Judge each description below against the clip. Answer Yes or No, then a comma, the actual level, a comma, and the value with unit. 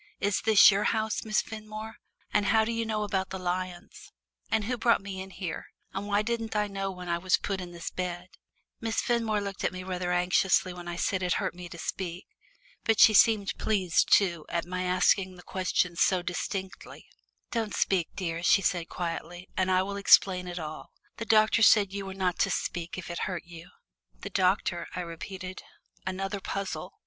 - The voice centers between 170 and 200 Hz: Yes, high, 190 Hz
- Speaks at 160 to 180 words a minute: No, average, 195 wpm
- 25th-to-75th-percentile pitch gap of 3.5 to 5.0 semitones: No, average, 2.7 semitones